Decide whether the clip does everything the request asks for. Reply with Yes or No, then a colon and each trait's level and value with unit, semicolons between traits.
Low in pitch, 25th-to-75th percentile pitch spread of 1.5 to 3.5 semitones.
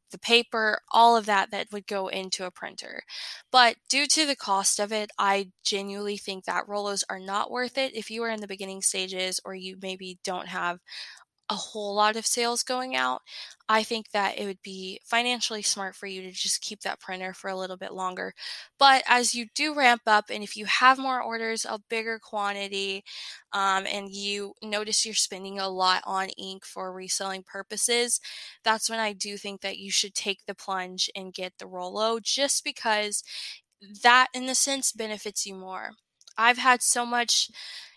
No: high, 205 Hz; average, 3.1 semitones